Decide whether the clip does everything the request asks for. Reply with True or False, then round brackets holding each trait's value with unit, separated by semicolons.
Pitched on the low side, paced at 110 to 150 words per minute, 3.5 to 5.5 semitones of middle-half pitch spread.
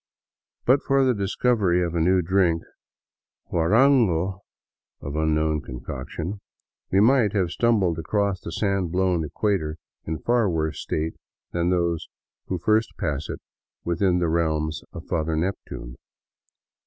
True (85 Hz; 140 wpm; 3.9 semitones)